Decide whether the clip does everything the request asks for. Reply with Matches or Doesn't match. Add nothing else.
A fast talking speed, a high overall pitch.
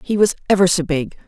Doesn't match